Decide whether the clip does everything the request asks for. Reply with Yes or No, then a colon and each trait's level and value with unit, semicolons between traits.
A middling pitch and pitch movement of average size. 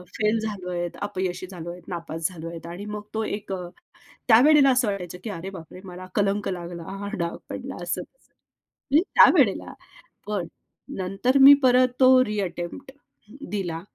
No: high, 195 Hz; average, 3.8 semitones